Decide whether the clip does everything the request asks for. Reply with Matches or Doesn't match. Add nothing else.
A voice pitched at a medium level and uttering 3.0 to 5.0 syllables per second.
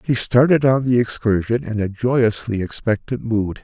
Doesn't match